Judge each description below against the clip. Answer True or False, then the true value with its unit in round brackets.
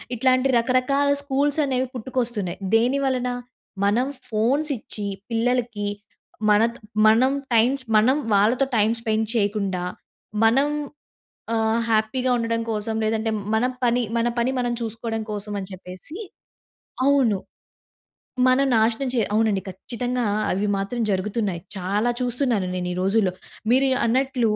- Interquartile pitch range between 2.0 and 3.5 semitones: True (3.2 semitones)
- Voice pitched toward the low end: False (230 Hz)